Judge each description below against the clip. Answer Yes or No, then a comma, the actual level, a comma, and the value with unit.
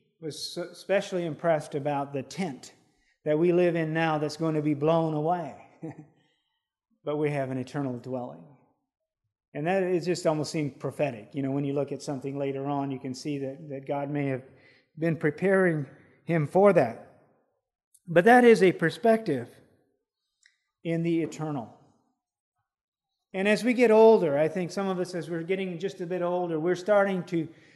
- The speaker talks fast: No, average, 175 wpm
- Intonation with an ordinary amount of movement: Yes, average, 4.1 semitones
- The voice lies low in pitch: No, medium, 160 Hz